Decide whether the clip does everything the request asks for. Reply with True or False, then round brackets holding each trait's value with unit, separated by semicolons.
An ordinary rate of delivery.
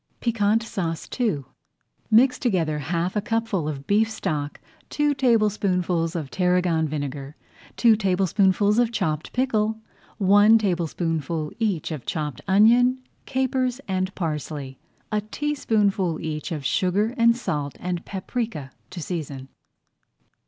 False (120 wpm)